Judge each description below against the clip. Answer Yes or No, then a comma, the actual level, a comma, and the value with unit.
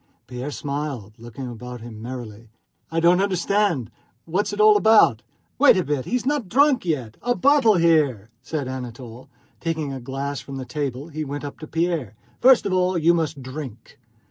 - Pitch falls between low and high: Yes, medium, 145 Hz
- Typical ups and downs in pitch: No, wide, 6.3 semitones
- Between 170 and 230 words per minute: Yes, average, 185 wpm